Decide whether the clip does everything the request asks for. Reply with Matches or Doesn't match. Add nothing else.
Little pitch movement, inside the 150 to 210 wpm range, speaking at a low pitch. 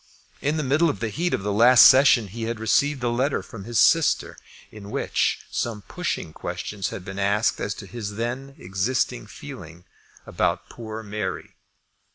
Doesn't match